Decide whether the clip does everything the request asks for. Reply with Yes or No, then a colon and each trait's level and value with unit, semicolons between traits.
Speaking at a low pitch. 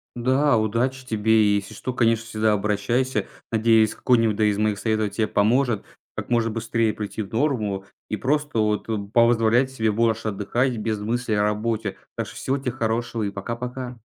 Yes: low, 115 Hz